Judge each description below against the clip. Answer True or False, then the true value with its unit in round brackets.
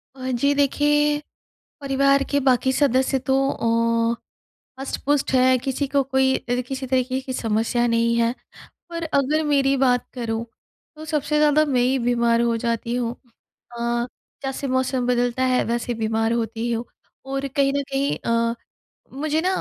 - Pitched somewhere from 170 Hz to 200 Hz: False (260 Hz)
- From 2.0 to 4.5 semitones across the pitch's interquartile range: True (2.8 semitones)